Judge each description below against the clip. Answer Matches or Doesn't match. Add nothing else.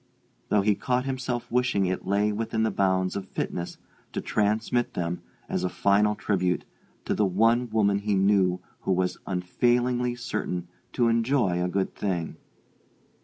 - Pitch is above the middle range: Doesn't match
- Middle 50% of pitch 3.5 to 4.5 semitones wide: Matches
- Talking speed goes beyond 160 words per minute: Doesn't match